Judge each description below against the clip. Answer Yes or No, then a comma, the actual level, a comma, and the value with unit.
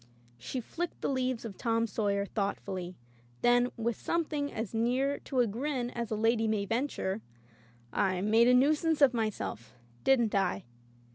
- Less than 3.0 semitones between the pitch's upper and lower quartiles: No, average, 4.2 semitones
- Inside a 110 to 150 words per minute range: No, average, 160 wpm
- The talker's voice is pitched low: No, high, 230 Hz